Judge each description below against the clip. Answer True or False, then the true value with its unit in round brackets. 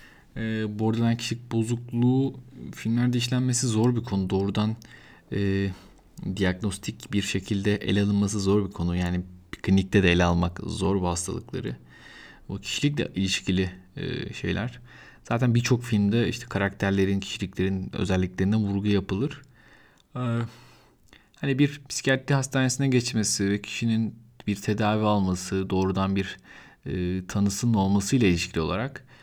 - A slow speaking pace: False (125 wpm)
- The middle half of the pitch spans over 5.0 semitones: False (3.6 semitones)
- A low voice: True (105 Hz)